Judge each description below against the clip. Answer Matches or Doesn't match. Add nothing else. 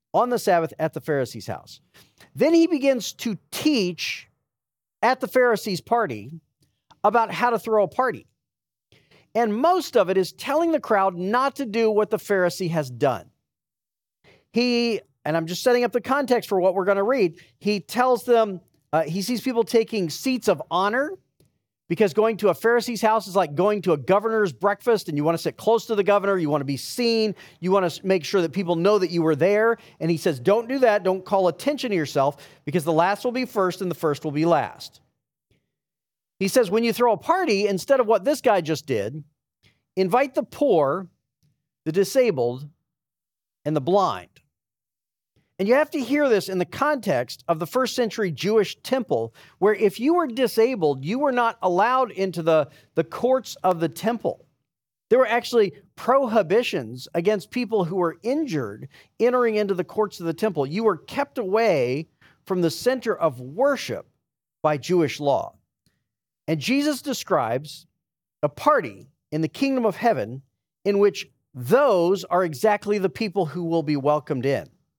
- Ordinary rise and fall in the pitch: Doesn't match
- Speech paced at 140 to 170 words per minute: Doesn't match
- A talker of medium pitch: Doesn't match